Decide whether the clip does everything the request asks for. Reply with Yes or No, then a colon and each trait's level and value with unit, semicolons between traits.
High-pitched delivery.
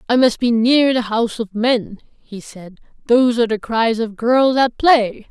Yes: high, 235 Hz